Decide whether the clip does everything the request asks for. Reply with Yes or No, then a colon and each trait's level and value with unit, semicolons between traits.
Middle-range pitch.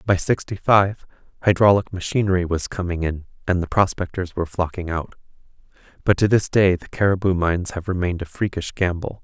No: very low, 90 Hz